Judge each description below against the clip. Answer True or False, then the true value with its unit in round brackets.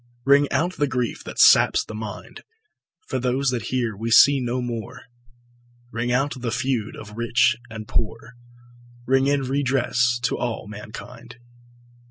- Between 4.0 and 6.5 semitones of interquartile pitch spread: False (2.4 semitones)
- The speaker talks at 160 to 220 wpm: False (150 wpm)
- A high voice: False (125 Hz)